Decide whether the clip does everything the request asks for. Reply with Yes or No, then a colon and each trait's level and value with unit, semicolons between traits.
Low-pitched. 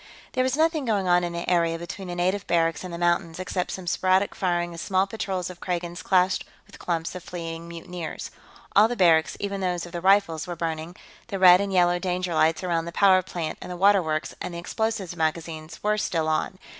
No: medium, 175 Hz